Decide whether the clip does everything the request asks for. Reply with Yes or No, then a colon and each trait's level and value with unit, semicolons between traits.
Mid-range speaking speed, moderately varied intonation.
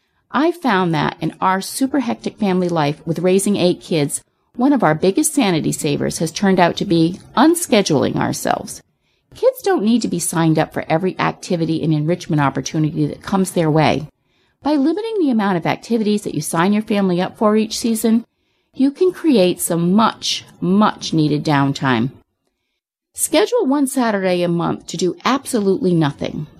No: average, 170 wpm; wide, 6.6 semitones